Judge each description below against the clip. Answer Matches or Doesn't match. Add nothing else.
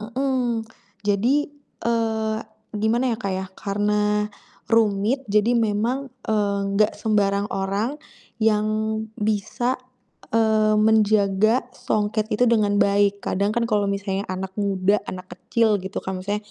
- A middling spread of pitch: Doesn't match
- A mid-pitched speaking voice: Doesn't match